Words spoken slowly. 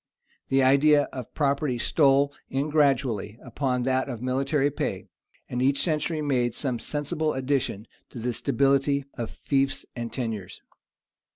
No: average, 145 wpm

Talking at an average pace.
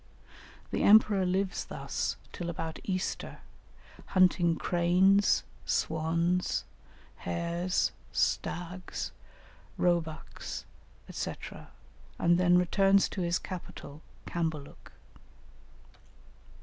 No: slow, 75 wpm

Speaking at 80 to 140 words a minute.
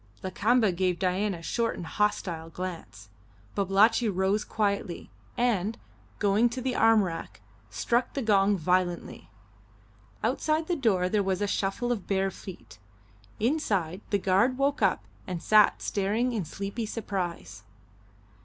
Yes: slow, 135 wpm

